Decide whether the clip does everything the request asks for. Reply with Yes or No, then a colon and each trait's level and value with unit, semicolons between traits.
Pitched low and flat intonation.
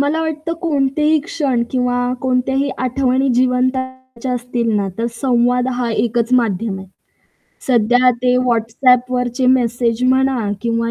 No: very high, 250 Hz; narrow, 1.8 semitones